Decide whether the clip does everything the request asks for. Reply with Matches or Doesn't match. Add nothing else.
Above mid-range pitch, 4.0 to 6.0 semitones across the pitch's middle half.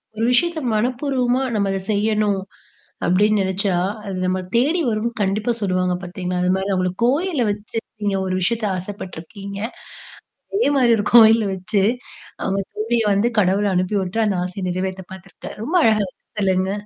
Doesn't match